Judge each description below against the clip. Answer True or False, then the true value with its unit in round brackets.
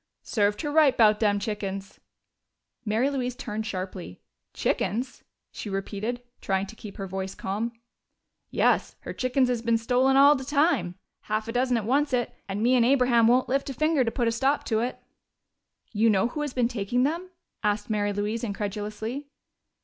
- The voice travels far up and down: False (3.8 semitones)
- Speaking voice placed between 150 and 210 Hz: False (230 Hz)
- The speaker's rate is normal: True (175 wpm)